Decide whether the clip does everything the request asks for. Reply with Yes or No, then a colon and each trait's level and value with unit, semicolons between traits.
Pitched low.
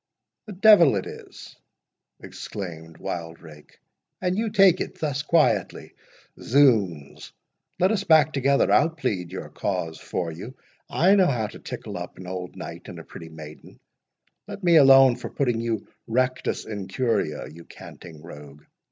Yes: low, 115 Hz